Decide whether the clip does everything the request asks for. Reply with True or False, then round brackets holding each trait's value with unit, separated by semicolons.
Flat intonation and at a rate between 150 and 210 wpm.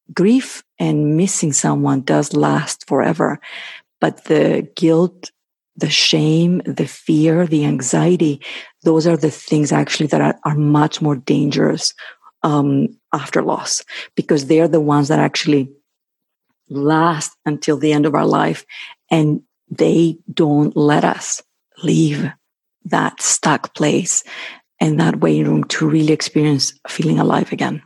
False (2.0 semitones; 135 wpm)